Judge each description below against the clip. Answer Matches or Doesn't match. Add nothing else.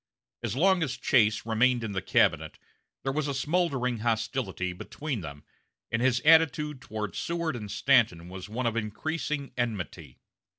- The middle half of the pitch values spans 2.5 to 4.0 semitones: Doesn't match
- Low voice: Matches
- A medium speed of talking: Matches